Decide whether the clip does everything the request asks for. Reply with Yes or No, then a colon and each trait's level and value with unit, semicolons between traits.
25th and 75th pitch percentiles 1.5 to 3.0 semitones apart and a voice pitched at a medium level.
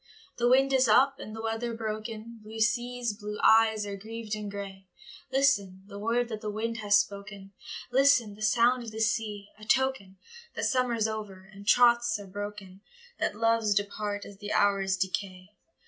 No: narrow, 2.5 semitones; high, 215 Hz